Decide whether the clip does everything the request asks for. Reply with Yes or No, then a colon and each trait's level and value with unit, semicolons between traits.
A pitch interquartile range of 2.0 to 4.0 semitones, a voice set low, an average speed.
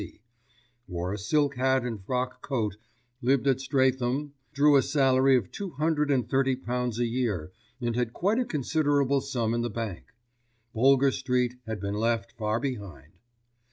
Yes: average, 3.2 semitones; low, 125 Hz; average, 165 wpm